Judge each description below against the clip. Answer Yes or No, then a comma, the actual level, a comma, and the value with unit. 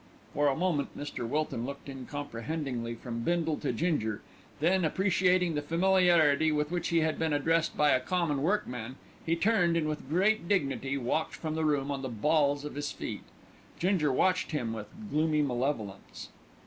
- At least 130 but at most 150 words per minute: No, average, 170 wpm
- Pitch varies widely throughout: No, average, 3.7 semitones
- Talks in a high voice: No, medium, 150 Hz